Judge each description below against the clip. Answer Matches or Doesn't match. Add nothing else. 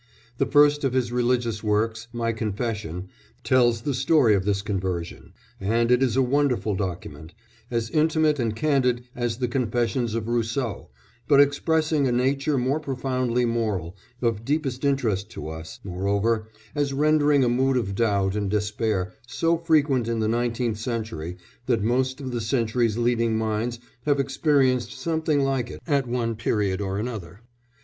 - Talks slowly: Doesn't match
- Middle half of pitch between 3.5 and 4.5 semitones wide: Matches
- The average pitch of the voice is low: Matches